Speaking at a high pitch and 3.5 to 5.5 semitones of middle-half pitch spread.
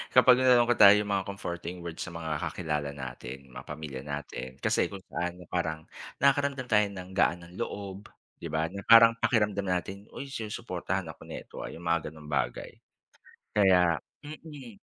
No: very low, 95 Hz; average, 5.1 semitones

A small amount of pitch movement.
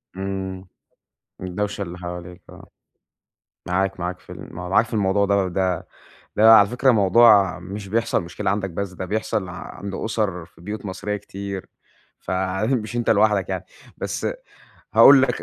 Yes: narrow, 2.2 semitones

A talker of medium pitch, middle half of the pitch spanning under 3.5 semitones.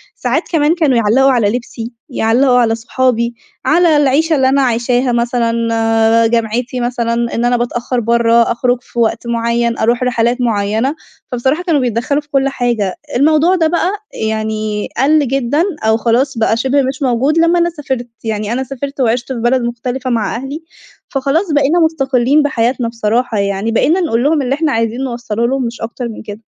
No: high, 245 Hz; average, 3.0 semitones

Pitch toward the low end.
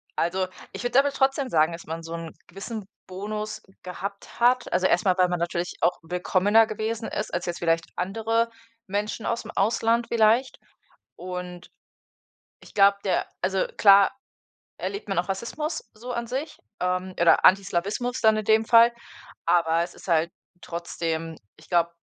No: high, 195 Hz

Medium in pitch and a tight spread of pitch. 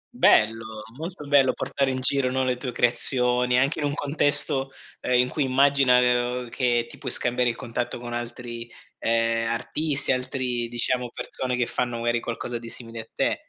No: low, 125 Hz; narrow, 2.0 semitones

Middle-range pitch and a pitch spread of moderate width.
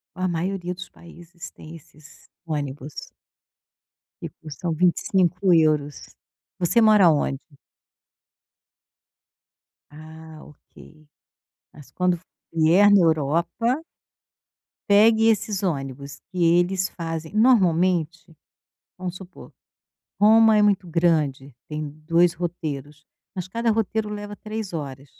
Yes: medium, 175 Hz; average, 3.8 semitones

